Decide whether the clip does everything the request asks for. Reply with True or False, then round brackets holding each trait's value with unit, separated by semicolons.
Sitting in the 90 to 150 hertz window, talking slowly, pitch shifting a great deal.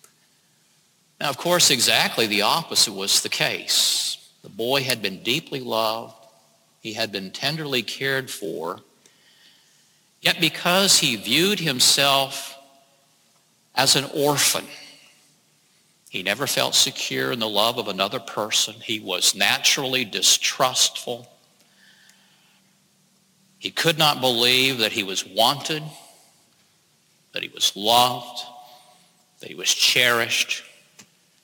True (135 Hz; 110 wpm; 6.4 semitones)